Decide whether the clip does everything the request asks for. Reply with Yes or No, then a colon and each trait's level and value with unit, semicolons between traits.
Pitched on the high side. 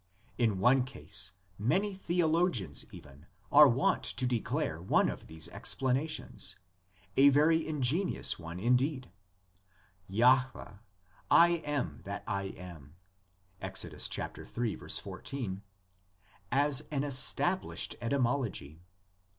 No: low, 125 Hz